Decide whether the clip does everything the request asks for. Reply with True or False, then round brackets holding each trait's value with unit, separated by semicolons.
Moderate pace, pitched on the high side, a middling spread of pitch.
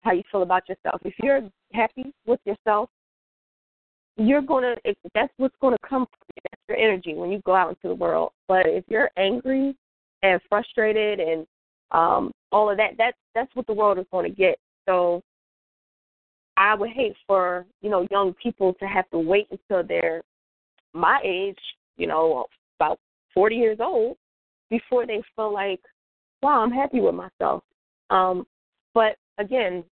True (170 wpm; 210 Hz; 4.6 semitones)